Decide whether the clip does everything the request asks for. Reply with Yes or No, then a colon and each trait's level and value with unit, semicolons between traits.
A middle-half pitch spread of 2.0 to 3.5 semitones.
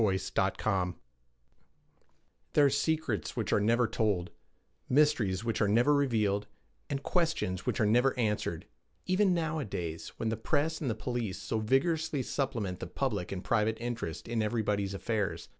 No: wide, 5.4 semitones